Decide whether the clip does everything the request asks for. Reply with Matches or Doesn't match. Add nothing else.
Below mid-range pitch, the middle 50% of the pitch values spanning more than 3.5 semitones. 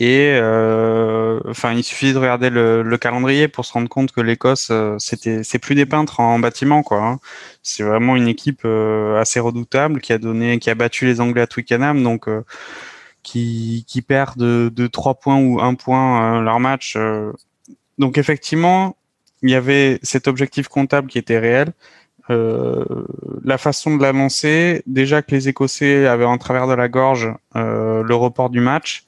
Doesn't match